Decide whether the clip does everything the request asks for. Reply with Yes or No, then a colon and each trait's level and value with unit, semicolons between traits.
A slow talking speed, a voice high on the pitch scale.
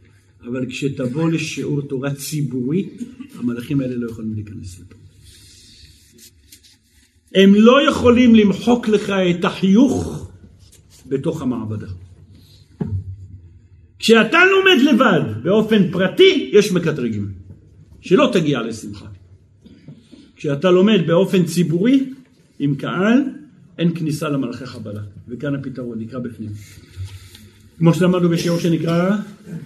No: slow, 95 wpm; low, 135 Hz